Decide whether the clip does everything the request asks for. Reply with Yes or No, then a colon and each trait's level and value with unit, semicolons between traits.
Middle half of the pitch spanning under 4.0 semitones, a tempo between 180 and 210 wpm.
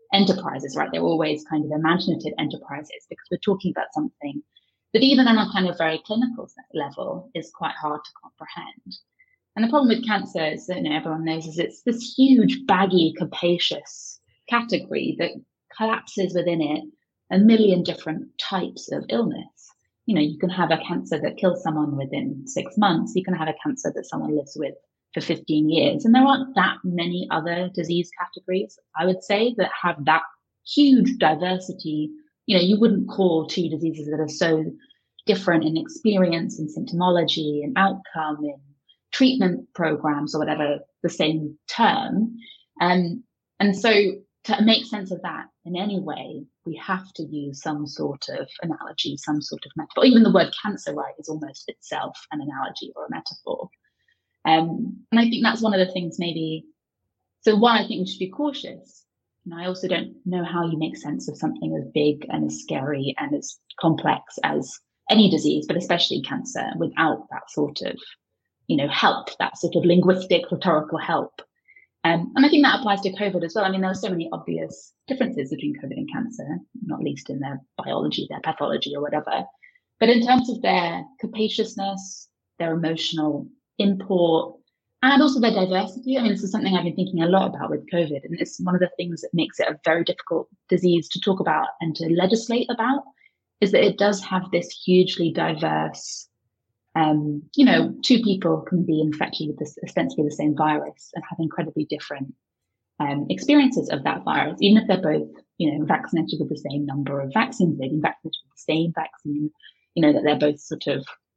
No: wide, 5.4 semitones; average, 185 wpm